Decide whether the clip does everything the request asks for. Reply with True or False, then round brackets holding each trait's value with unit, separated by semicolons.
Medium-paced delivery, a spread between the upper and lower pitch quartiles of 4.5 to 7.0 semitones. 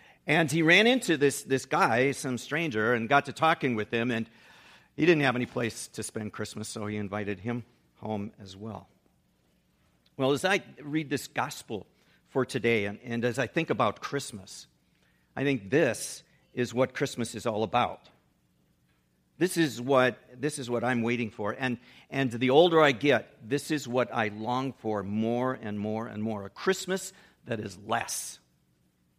True (175 wpm; 4.8 semitones)